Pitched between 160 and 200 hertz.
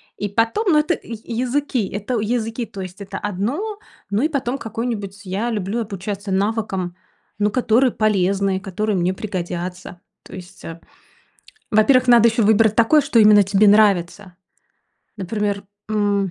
No: high, 210 Hz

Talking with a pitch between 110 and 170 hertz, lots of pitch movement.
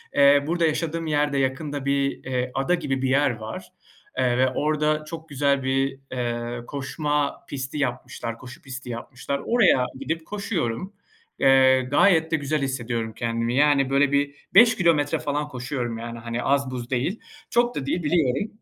No: medium, 140 Hz; average, 3.2 semitones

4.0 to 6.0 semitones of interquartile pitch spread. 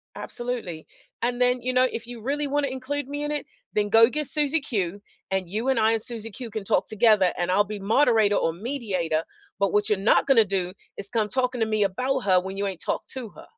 Yes: average, 4.4 semitones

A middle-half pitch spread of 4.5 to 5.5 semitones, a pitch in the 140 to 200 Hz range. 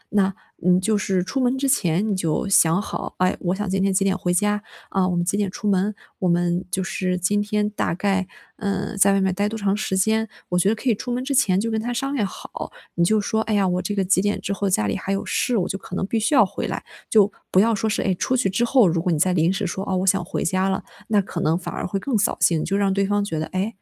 No: narrow, 2.4 semitones; high, 195 Hz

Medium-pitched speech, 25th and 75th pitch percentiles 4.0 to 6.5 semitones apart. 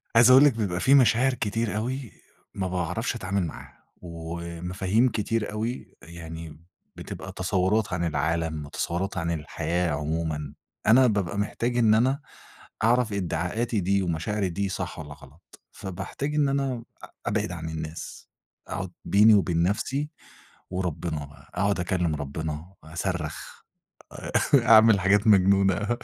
No: very low, 95 Hz; average, 4.9 semitones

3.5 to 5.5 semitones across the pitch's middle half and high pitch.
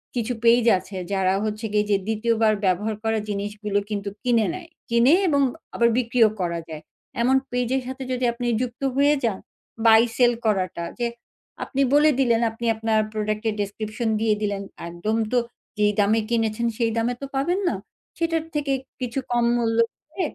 No: average, 2.9 semitones; high, 225 Hz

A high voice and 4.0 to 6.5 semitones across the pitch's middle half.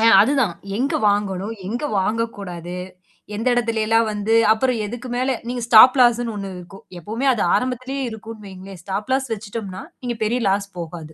No: high, 220 Hz; average, 3.6 semitones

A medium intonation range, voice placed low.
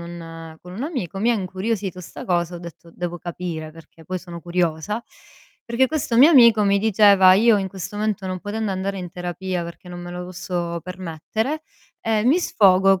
No: average, 3.4 semitones; medium, 185 Hz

